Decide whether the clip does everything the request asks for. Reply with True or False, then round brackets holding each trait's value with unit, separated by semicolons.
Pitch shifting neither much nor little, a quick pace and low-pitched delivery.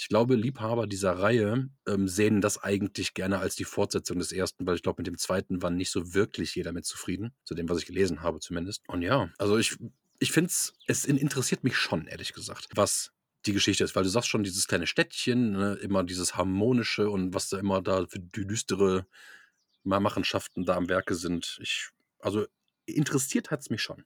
True (4.1 semitones; 205 wpm; 100 Hz)